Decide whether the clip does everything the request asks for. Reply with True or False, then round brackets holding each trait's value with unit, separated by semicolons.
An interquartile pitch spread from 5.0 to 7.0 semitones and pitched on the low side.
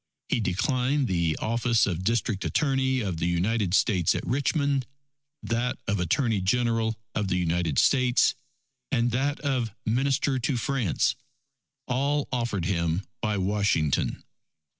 True (5.6 semitones; 115 Hz)